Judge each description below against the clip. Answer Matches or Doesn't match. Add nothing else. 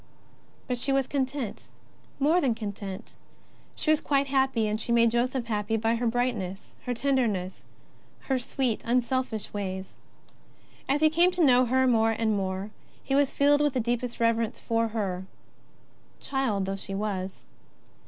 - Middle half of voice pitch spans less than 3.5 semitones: Doesn't match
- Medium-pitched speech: Doesn't match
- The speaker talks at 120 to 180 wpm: Matches